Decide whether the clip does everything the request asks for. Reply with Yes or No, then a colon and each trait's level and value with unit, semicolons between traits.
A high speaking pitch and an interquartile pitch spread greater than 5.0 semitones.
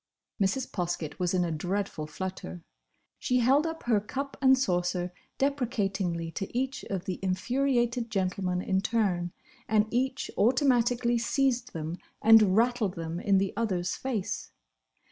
Yes: high, 205 Hz; wide, 5.4 semitones